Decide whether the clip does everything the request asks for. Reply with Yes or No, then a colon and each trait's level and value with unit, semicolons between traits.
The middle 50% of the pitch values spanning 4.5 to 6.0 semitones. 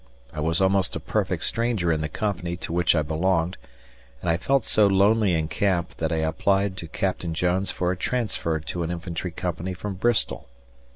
No: average, 3.0 semitones